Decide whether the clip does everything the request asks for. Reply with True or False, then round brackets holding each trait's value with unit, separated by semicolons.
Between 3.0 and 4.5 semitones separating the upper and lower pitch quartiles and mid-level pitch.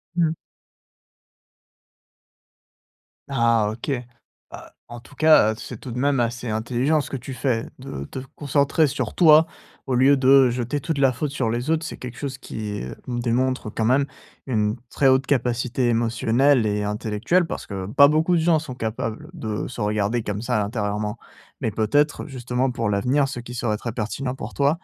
False (3.9 semitones; 125 Hz)